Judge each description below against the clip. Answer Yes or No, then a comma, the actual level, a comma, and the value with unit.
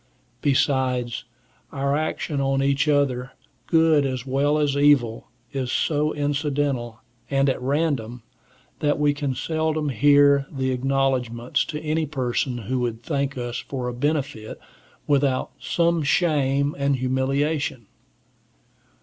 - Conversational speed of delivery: No, slow, 125 wpm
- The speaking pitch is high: No, medium, 140 Hz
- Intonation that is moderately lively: No, narrow, 2.2 semitones